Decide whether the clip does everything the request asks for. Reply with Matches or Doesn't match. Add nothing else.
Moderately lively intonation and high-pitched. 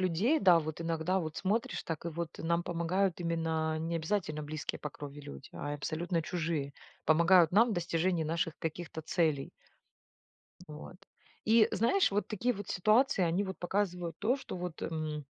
Doesn't match